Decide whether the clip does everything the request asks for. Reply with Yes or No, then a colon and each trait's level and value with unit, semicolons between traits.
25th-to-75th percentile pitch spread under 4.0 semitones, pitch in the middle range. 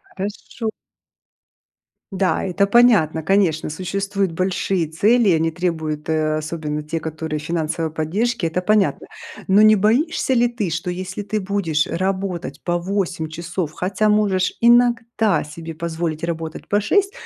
No: average, 4.3 semitones; medium, 180 Hz